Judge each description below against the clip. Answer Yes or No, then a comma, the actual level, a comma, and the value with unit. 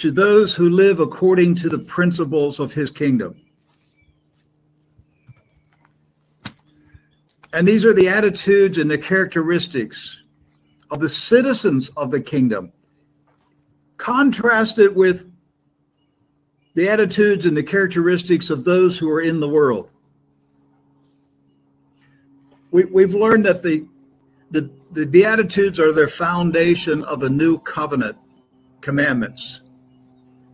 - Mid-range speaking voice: Yes, medium, 155 Hz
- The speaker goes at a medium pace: No, slow, 110 wpm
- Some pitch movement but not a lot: No, wide, 5.8 semitones